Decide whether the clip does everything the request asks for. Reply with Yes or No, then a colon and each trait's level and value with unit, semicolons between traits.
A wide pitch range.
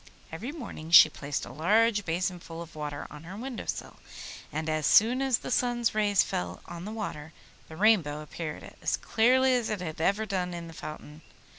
Yes: wide, 6.1 semitones